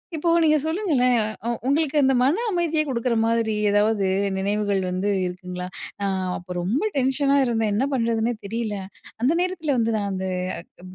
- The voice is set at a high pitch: Yes, high, 235 Hz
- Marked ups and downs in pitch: Yes, wide, 5.7 semitones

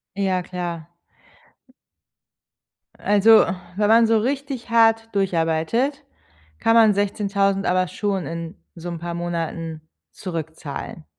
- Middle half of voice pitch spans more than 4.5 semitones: Yes, average, 4.9 semitones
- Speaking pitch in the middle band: No, high, 195 Hz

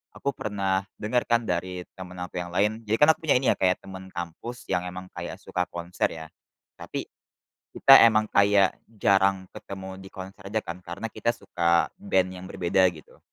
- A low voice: Yes, very low, 95 Hz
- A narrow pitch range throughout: No, average, 3.1 semitones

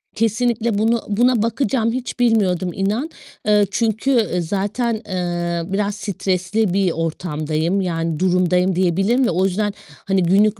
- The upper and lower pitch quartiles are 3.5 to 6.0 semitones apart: Yes, average, 3.8 semitones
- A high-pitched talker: Yes, high, 195 Hz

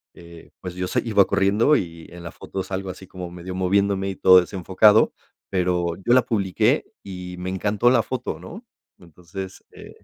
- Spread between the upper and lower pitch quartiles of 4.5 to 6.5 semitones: No, narrow, 2.4 semitones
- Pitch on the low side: Yes, very low, 95 Hz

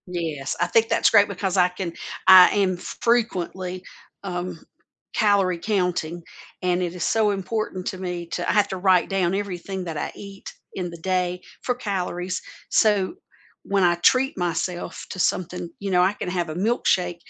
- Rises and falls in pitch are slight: Yes, narrow, 2.0 semitones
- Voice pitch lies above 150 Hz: Yes, medium, 185 Hz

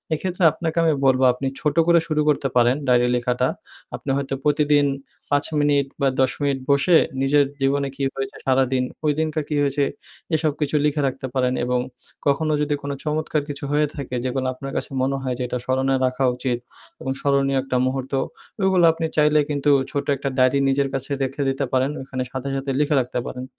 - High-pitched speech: No, medium, 140 Hz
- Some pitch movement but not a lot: No, narrow, 2.1 semitones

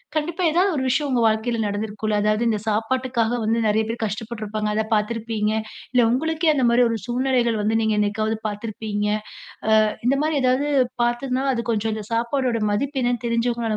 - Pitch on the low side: No, high, 230 Hz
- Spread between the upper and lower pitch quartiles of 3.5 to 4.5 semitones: No, average, 2.9 semitones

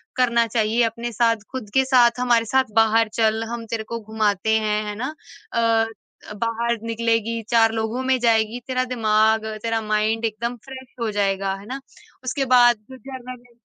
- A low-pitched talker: No, high, 230 Hz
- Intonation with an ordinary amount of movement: No, narrow, 1.9 semitones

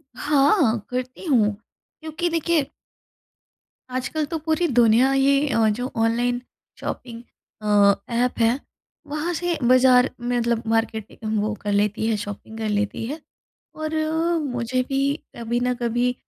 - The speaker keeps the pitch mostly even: No, average, 3.8 semitones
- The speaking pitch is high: Yes, high, 245 Hz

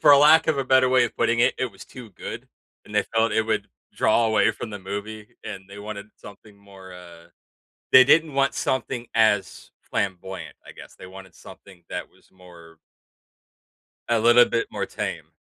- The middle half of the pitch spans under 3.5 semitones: No, average, 4.1 semitones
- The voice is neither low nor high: No, low, 110 Hz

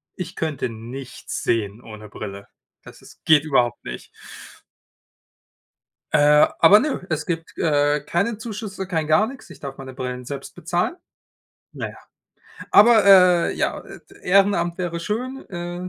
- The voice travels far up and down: Yes, wide, 6.1 semitones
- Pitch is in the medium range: Yes, medium, 165 Hz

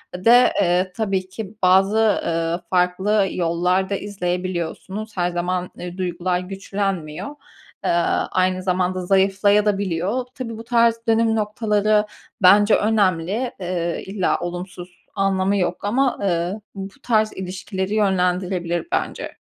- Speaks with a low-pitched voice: No, high, 190 Hz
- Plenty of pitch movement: No, average, 2.7 semitones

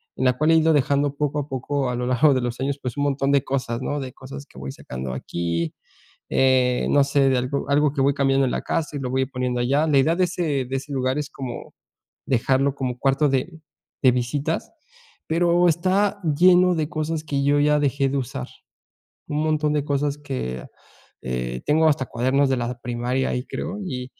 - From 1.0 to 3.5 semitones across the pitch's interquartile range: Yes, average, 2.8 semitones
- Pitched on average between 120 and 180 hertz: Yes, medium, 140 Hz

